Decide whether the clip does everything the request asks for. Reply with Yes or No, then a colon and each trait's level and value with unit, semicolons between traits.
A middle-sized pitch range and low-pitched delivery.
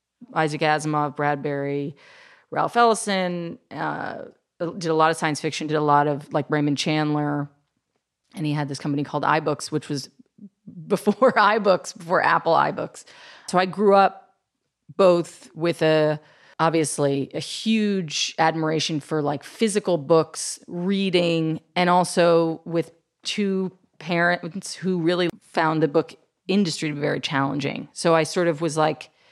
No: average, 3.4 semitones; medium, 165 Hz